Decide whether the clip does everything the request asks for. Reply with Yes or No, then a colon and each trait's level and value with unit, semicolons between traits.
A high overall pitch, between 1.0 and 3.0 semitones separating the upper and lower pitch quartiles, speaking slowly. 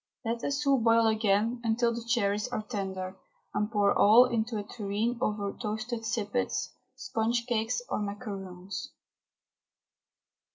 Yes: high, 220 Hz; narrow, 2.5 semitones; slow, 130 wpm